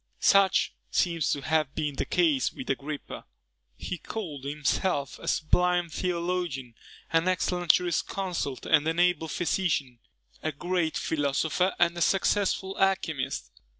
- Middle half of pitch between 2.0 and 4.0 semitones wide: Yes, average, 3.6 semitones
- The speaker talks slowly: Yes, slow, 120 wpm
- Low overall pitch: No, medium, 170 Hz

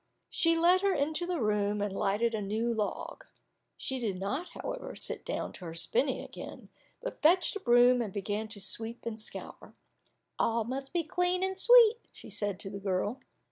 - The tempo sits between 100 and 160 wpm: No, average, 185 wpm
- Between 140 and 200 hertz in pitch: No, high, 235 Hz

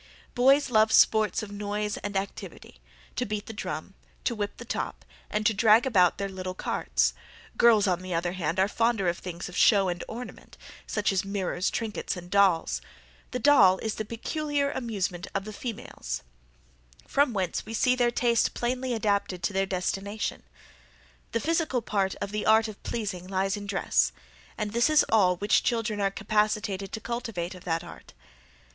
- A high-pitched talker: Yes, high, 205 Hz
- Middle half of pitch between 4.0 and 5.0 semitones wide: No, average, 3.4 semitones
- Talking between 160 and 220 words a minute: Yes, average, 175 wpm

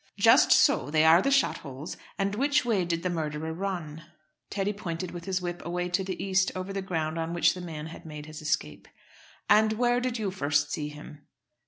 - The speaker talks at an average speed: No, fast, 210 wpm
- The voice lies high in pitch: No, medium, 175 Hz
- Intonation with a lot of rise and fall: No, average, 4.0 semitones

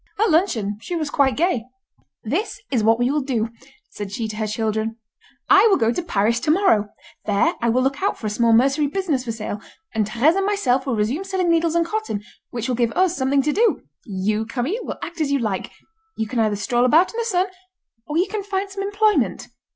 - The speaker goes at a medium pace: No, fast, 225 wpm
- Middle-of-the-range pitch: No, very high, 265 Hz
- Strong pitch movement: Yes, wide, 8.2 semitones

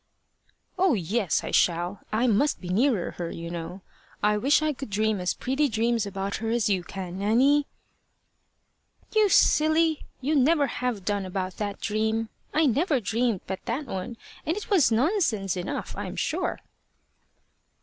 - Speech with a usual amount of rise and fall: No, wide, 6.4 semitones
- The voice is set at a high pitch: Yes, high, 225 Hz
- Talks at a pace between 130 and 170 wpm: Yes, average, 160 wpm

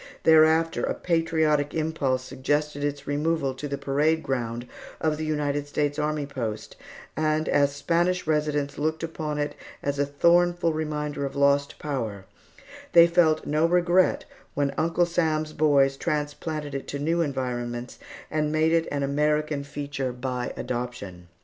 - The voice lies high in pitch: No, medium, 150 Hz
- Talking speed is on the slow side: No, average, 145 wpm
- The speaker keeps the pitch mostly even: Yes, narrow, 2.1 semitones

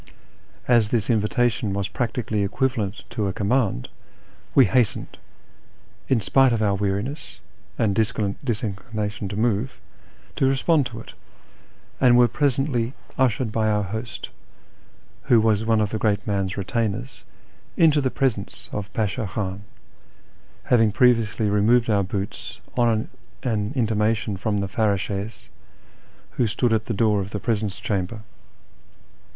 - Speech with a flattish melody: No, average, 3.1 semitones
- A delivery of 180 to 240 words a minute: No, slow, 135 wpm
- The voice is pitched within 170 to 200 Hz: No, low, 110 Hz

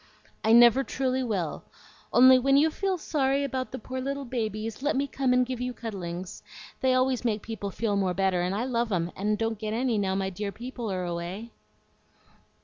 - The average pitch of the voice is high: Yes, high, 230 Hz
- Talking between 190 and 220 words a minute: Yes, average, 200 wpm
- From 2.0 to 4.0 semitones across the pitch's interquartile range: No, average, 4.5 semitones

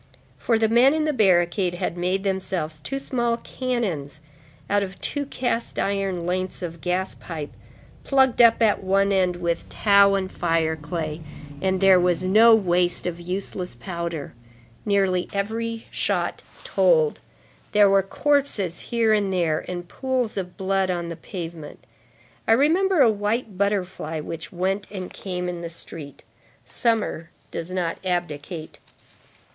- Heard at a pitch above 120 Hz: Yes, high, 190 Hz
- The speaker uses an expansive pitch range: No, average, 4.0 semitones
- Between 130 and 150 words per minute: Yes, average, 145 wpm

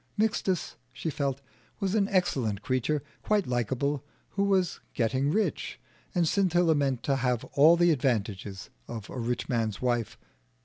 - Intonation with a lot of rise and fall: Yes, wide, 6.5 semitones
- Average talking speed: Yes, average, 145 wpm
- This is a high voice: No, medium, 140 Hz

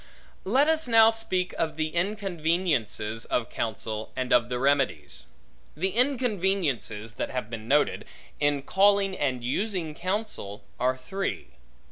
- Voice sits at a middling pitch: Yes, medium, 155 Hz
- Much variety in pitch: Yes, wide, 8.1 semitones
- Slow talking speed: Yes, slow, 130 wpm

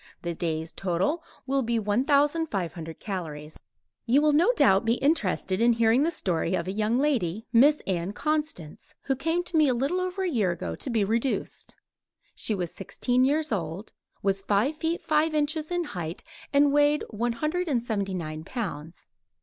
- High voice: Yes, high, 235 Hz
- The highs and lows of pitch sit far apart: Yes, wide, 8.0 semitones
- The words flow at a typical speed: Yes, average, 175 wpm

